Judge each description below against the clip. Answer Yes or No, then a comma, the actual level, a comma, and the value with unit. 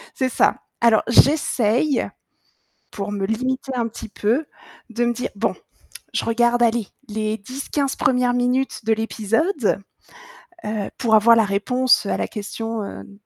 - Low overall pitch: No, high, 230 Hz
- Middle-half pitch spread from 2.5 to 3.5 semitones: Yes, average, 2.8 semitones